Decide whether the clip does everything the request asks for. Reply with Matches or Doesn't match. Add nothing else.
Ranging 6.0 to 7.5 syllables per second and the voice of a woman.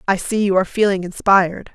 Matches